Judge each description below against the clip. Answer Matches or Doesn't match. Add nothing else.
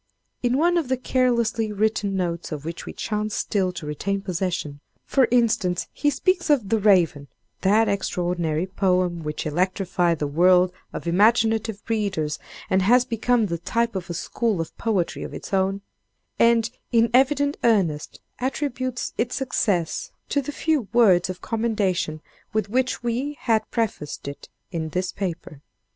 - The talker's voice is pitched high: Matches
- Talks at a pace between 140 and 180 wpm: Matches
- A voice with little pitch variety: Doesn't match